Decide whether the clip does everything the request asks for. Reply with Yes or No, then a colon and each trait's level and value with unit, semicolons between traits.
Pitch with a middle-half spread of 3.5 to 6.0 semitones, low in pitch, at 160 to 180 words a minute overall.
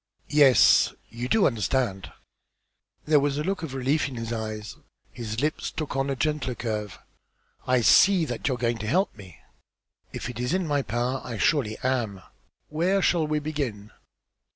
Yes: average, 5.1 semitones; low, 130 Hz; average, 175 wpm